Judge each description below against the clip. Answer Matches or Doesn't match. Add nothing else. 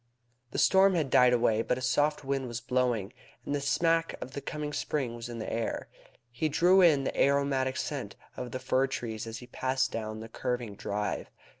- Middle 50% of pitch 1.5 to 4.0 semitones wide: Matches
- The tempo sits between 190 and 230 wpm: Matches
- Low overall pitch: Matches